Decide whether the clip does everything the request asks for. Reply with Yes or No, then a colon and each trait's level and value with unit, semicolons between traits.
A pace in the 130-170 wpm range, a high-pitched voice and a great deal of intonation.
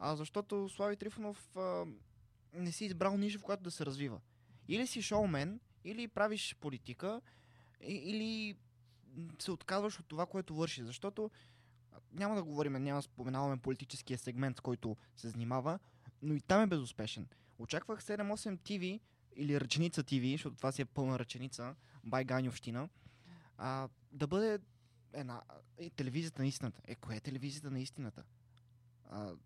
No: average, 150 wpm; medium, 140 Hz; wide, 7.5 semitones